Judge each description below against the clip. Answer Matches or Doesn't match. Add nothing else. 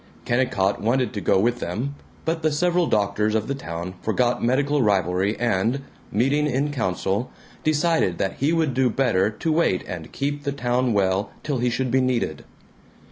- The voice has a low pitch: Matches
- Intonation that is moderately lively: Doesn't match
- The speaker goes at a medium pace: Matches